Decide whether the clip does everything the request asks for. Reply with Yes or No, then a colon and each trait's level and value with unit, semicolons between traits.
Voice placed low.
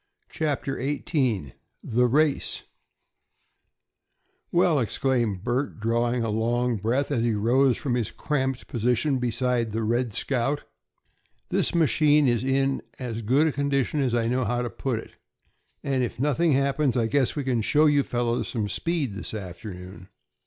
Yes: low, 125 Hz